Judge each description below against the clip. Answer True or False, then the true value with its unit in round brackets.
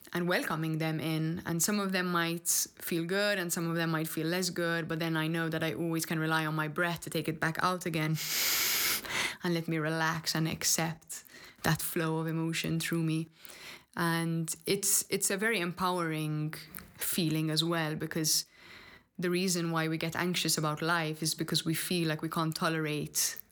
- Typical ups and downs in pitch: False (1.4 semitones)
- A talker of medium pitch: True (165 Hz)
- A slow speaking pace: False (190 wpm)